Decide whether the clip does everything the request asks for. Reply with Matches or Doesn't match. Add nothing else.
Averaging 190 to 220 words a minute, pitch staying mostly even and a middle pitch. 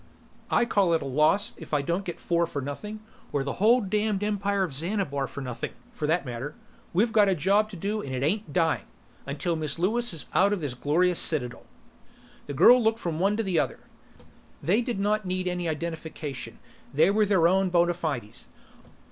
Doesn't match